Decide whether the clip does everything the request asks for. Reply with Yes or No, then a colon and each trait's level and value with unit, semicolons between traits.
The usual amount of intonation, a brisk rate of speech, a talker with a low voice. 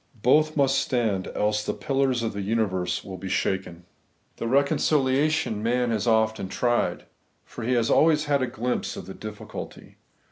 No: average, 4.3 semitones; average, 165 wpm; low, 115 Hz